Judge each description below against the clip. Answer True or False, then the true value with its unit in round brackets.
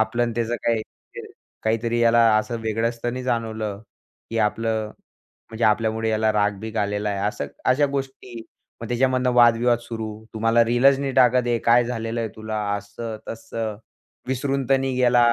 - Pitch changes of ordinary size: False (1.8 semitones)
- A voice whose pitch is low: True (115 Hz)